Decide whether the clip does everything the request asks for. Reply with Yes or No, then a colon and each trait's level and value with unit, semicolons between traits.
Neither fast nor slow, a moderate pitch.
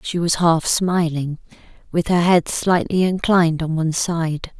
Yes: average, 155 wpm; medium, 170 Hz